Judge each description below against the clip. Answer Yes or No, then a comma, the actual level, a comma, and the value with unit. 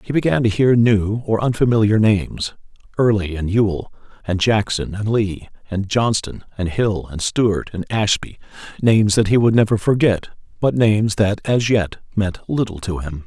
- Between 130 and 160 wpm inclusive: No, average, 170 wpm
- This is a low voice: Yes, low, 105 Hz